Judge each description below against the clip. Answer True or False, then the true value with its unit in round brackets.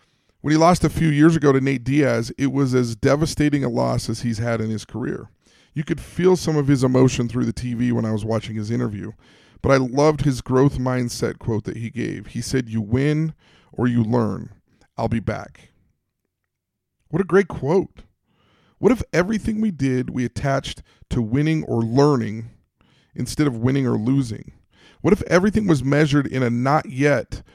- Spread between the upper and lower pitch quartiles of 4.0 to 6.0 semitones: True (4.3 semitones)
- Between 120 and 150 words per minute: False (190 wpm)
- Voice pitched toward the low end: True (130 Hz)